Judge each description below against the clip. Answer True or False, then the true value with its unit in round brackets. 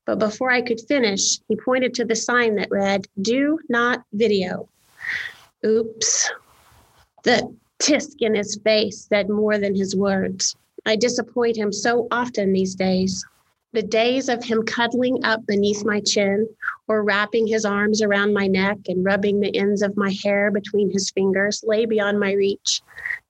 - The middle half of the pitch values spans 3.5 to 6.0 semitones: False (2.8 semitones)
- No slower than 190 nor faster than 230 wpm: False (160 wpm)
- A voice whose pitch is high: True (215 Hz)